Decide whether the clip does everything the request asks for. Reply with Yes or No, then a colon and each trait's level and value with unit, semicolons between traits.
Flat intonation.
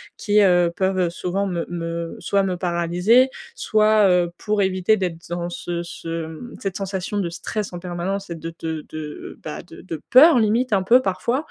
No: average, 3.2 semitones